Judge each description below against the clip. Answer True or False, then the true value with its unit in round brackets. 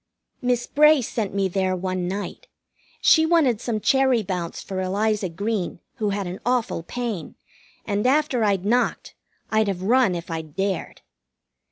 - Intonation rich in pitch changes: False (4.8 semitones)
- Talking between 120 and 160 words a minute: True (155 wpm)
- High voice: True (205 Hz)